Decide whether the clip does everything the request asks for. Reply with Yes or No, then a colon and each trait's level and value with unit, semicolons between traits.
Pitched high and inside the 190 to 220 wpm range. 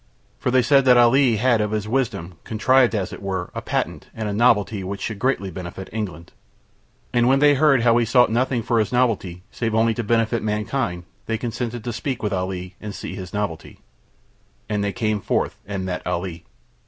No: low, 110 Hz; average, 200 wpm